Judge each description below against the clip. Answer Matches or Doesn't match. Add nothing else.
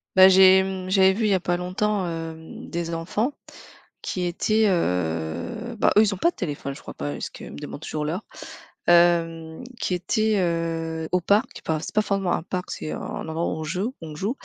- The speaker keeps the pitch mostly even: Doesn't match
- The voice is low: Doesn't match